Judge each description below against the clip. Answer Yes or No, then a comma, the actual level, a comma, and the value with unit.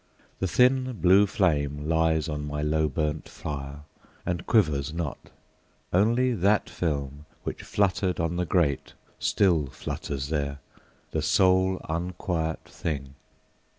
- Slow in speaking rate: Yes, slow, 120 wpm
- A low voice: Yes, very low, 80 Hz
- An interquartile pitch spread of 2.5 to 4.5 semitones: Yes, average, 4.2 semitones